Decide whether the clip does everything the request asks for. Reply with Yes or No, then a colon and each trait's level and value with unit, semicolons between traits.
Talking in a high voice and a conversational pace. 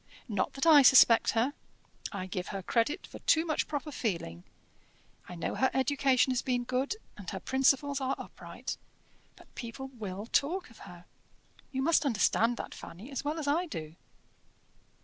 Yes: very high, 255 Hz; average, 170 wpm